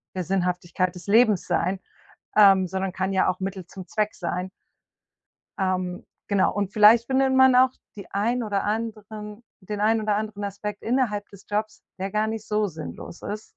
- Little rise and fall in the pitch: Yes, narrow, 2.3 semitones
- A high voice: Yes, high, 205 Hz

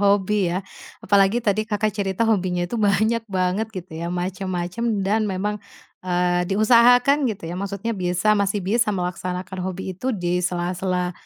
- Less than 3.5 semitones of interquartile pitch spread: Yes, average, 2.8 semitones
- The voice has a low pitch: No, high, 195 Hz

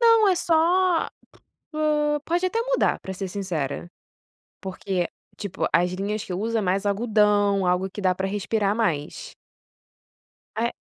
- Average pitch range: No, wide, 8.3 semitones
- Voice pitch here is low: No, high, 205 Hz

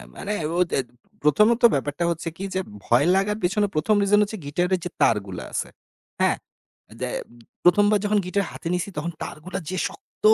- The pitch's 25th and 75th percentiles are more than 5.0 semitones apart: Yes, wide, 5.4 semitones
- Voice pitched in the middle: Yes, medium, 180 Hz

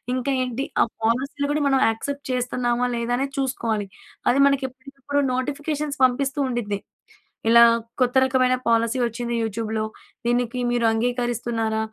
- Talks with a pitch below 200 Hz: No, high, 245 Hz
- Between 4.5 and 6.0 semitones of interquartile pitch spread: No, average, 2.7 semitones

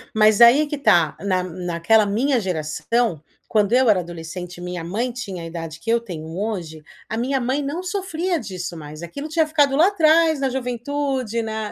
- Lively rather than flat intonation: Yes, wide, 7.8 semitones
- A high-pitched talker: Yes, high, 220 Hz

